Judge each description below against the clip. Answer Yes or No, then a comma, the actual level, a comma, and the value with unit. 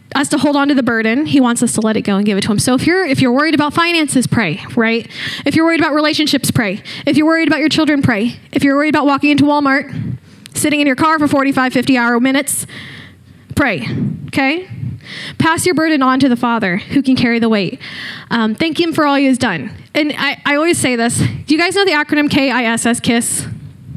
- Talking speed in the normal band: No, fast, 235 wpm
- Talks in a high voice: Yes, very high, 280 Hz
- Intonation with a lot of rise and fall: No, average, 4.1 semitones